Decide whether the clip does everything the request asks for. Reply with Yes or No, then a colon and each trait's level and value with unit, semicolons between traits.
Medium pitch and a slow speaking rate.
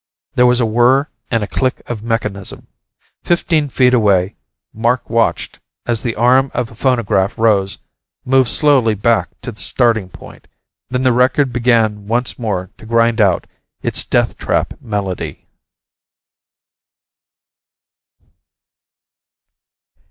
No: low, 115 Hz; slow, 125 wpm